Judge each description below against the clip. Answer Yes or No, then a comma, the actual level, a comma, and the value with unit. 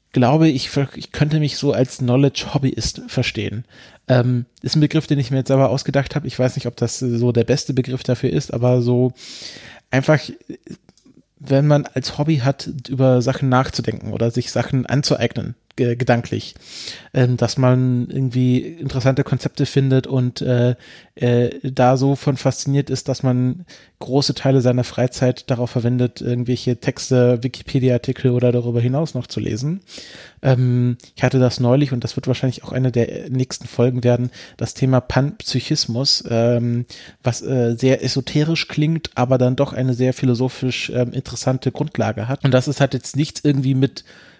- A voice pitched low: Yes, low, 130 Hz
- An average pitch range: No, narrow, 1.9 semitones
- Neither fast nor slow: Yes, average, 155 wpm